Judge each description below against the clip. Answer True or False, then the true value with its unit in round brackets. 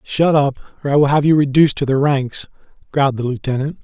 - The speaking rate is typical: False (220 wpm)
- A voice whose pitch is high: False (140 Hz)